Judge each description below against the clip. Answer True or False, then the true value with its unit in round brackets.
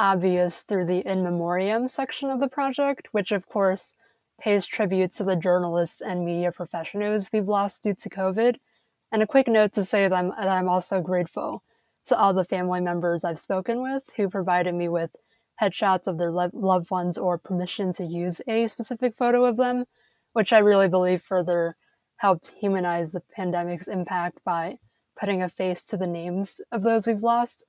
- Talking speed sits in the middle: True (185 wpm)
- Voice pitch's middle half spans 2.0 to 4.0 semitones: True (3.6 semitones)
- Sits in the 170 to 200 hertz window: True (190 Hz)